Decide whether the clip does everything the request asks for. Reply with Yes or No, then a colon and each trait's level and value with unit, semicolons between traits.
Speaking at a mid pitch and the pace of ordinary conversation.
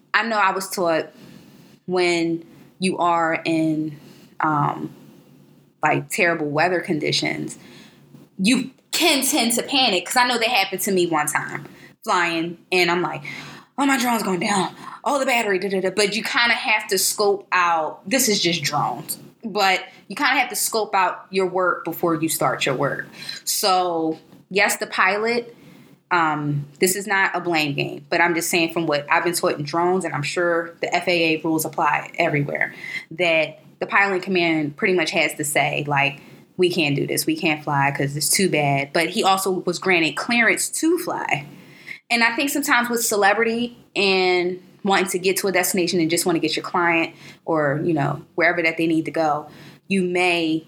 Yes: medium, 180 Hz; average, 190 wpm